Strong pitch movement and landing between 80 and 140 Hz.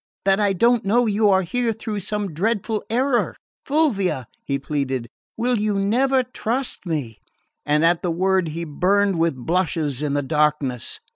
No: wide, 6.6 semitones; high, 190 Hz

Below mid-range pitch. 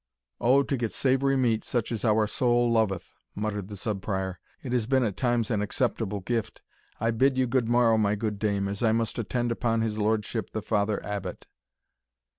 Yes: low, 110 Hz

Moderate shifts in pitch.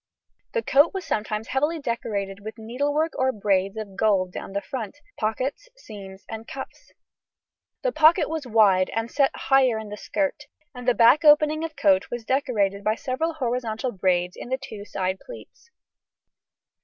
No: wide, 5.9 semitones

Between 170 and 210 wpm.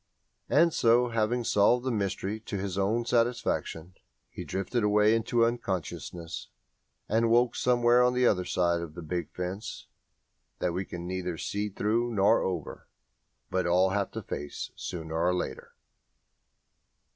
No: average, 150 wpm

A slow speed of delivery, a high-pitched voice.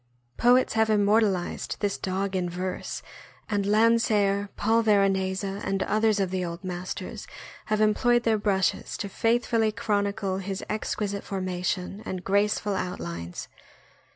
Yes: slow, 130 wpm; high, 200 Hz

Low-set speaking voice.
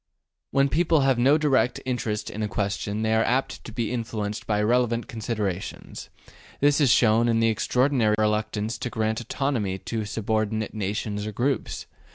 Yes: low, 110 Hz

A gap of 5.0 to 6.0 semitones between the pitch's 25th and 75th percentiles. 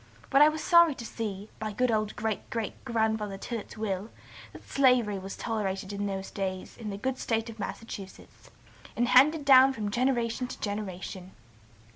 No: average, 3.8 semitones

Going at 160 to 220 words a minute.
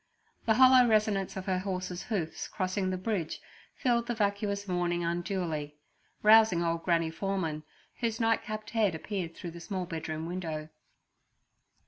No: average, 140 wpm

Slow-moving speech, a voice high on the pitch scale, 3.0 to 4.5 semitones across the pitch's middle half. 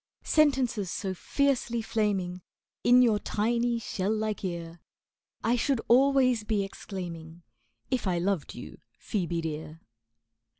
No: slow, 120 wpm; high, 210 Hz; average, 5.2 semitones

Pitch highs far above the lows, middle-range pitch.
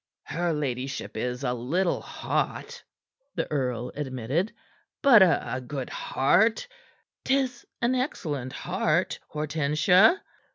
Yes: wide, 6.7 semitones; medium, 150 Hz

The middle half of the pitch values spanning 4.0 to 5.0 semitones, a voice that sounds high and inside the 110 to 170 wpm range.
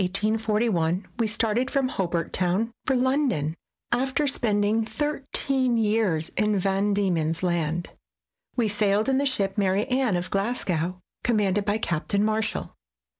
Yes: average, 4.6 semitones; high, 210 Hz; average, 140 wpm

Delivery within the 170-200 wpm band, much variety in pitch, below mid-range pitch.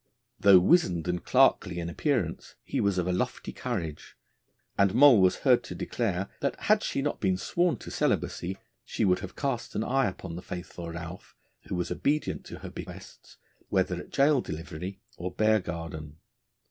Yes: average, 175 wpm; wide, 5.8 semitones; very low, 95 Hz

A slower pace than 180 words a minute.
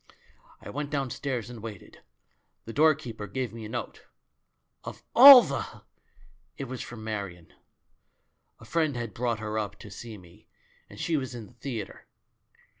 Yes: average, 160 wpm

